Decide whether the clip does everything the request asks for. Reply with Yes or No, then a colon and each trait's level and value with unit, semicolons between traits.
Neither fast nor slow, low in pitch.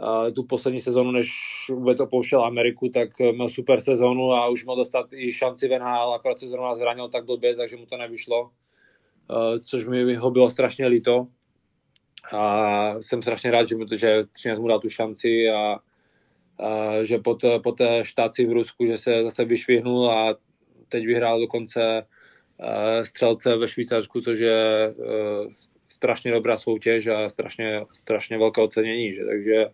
Yes: average, 155 wpm; low, 115 Hz